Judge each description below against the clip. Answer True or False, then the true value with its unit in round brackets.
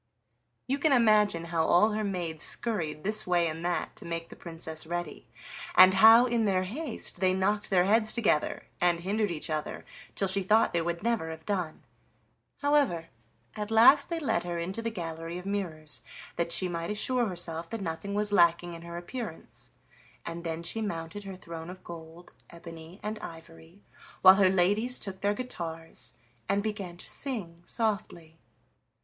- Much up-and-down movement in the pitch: False (4.1 semitones)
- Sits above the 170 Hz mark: True (185 Hz)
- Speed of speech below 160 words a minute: False (175 wpm)